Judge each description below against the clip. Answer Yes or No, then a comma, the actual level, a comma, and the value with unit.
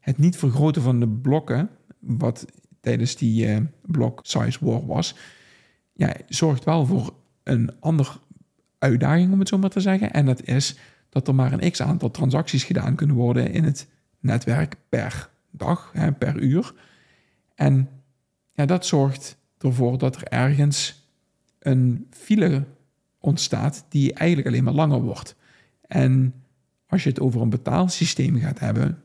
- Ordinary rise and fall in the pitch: Yes, average, 3.6 semitones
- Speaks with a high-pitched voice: No, medium, 140 Hz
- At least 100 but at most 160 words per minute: Yes, average, 155 wpm